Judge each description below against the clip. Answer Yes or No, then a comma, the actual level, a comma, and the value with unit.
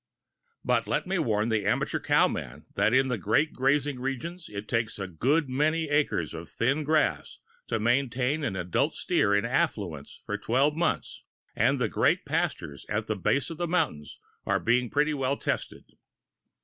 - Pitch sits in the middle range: No, low, 130 Hz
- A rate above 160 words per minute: Yes, average, 175 wpm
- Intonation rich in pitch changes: Yes, wide, 5.8 semitones